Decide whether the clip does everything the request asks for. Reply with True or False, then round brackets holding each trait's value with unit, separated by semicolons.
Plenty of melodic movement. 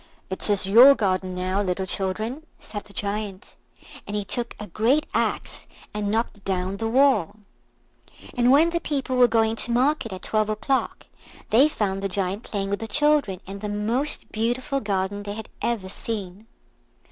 False (3.7 semitones)